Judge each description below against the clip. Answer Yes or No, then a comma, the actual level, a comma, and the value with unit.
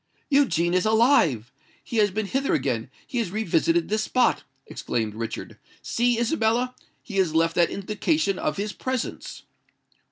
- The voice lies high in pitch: Yes, high, 210 Hz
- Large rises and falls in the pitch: Yes, wide, 6.0 semitones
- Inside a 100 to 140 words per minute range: Yes, slow, 135 wpm